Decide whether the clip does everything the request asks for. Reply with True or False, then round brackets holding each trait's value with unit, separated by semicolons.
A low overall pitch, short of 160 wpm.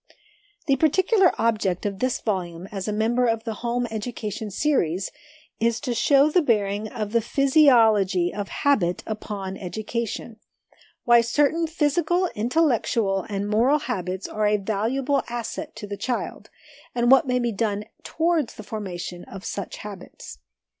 False (225 Hz; 145 wpm)